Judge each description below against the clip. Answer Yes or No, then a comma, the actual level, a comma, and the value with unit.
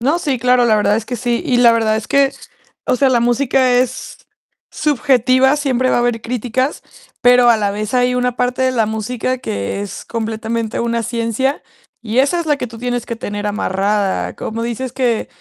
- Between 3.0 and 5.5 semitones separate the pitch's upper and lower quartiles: No, narrow, 2.5 semitones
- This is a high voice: Yes, high, 245 Hz